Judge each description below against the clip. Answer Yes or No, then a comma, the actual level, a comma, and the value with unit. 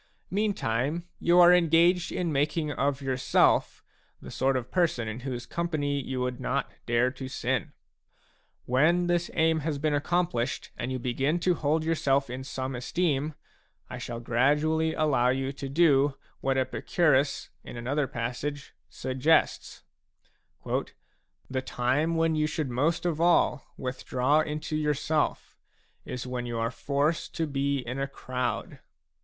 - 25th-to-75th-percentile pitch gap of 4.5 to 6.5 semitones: No, average, 3.8 semitones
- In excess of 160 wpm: No, average, 150 wpm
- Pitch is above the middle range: No, medium, 140 Hz